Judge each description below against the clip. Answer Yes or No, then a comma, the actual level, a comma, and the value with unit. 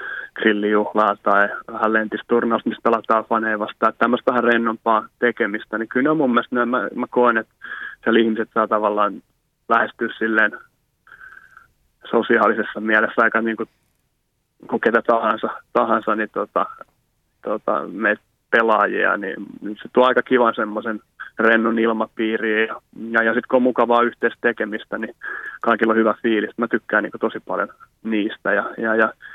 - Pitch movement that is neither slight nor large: No, narrow, 1.2 semitones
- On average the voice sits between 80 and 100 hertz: No, low, 115 Hz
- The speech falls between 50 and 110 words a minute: No, average, 150 wpm